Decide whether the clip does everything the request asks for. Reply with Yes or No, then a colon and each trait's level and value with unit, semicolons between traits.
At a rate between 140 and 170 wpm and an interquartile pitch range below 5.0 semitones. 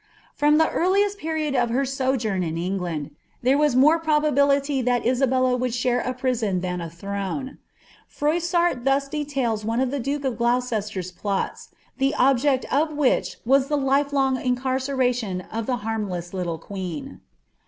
Yes: average, 155 wpm; average, 4.5 semitones